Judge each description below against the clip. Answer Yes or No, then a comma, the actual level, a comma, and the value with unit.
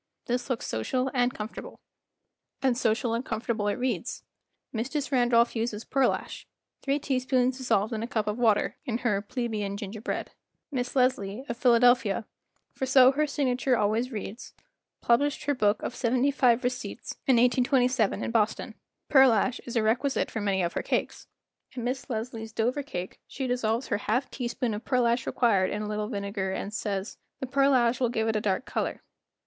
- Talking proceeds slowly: No, average, 175 wpm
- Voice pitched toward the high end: Yes, high, 240 Hz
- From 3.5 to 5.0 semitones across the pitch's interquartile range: No, average, 2.9 semitones